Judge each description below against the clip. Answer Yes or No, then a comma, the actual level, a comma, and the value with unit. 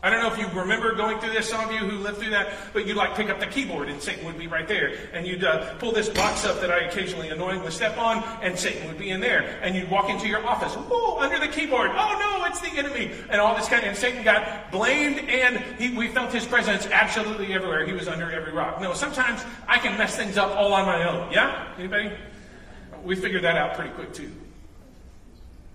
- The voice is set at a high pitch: Yes, high, 205 Hz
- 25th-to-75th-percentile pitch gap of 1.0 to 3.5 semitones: No, average, 4.1 semitones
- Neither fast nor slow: No, fast, 245 wpm